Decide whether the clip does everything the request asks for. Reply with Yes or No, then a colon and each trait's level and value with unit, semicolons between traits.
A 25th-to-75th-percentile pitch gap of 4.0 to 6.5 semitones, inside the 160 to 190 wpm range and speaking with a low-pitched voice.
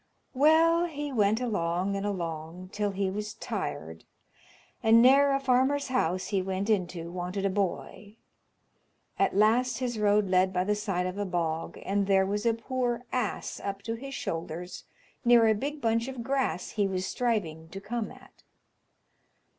No: average, 4.7 semitones; average, 165 wpm; high, 205 Hz